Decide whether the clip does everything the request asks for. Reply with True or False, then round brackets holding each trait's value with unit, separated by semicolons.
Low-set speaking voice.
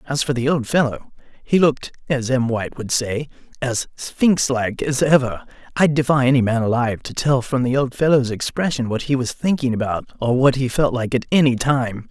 True (130 Hz)